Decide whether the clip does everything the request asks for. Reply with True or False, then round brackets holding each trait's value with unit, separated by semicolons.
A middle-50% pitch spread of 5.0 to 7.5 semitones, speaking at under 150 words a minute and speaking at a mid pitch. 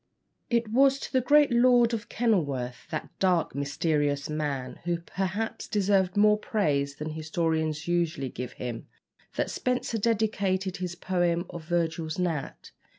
True (5.6 semitones; 140 wpm; 175 Hz)